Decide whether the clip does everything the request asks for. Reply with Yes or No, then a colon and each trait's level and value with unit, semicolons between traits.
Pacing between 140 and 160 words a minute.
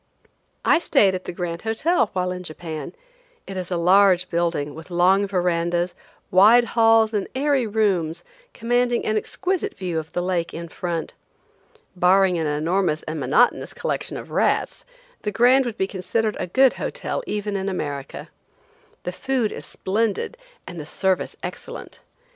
Yes: average, 155 wpm